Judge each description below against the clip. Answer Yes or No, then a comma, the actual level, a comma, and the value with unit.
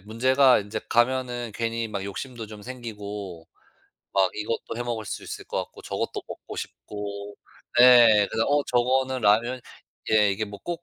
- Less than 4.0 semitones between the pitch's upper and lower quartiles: Yes, average, 3.2 semitones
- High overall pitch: No, low, 115 Hz